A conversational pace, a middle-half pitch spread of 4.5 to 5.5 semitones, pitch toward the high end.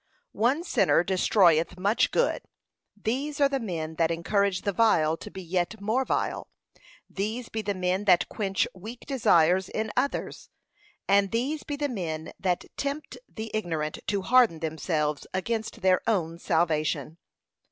Yes: average, 150 wpm; average, 5.2 semitones; high, 195 Hz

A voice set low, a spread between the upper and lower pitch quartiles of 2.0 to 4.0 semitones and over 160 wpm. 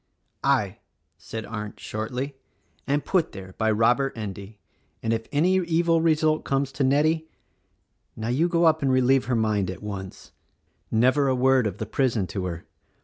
No: low, 125 Hz; wide, 5.4 semitones; average, 170 wpm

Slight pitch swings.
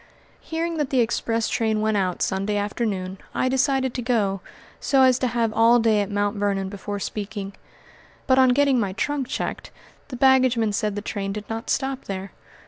No: average, 4.1 semitones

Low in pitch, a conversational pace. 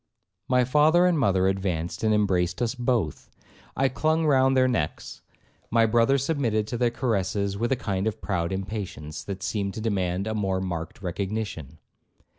Yes: low, 105 Hz; average, 165 wpm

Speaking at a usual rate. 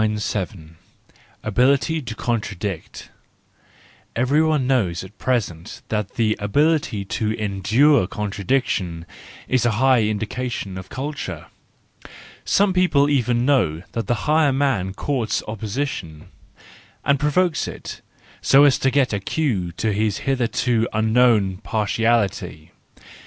No: slow, 115 wpm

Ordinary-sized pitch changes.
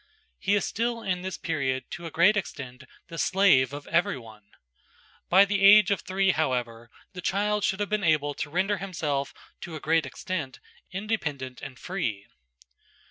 No: wide, 6.1 semitones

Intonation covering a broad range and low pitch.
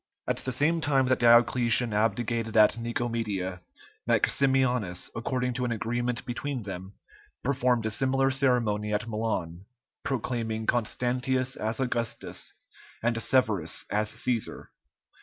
No: average, 2.7 semitones; low, 120 Hz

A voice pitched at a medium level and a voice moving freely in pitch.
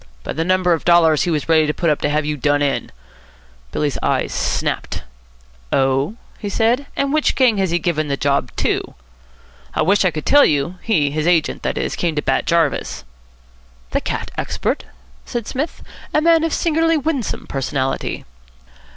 Yes: medium, 170 Hz; wide, 7.5 semitones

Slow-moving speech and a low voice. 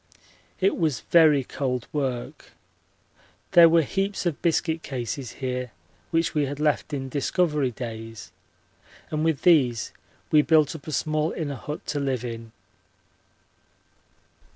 No: slow, 130 wpm; medium, 145 Hz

